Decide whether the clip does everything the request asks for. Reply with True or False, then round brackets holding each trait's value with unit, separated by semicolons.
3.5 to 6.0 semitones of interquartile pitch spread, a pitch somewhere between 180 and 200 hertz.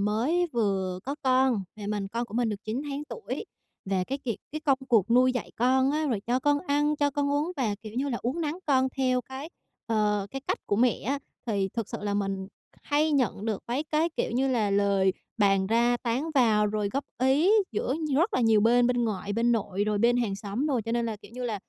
False (4.5 semitones; 240 Hz)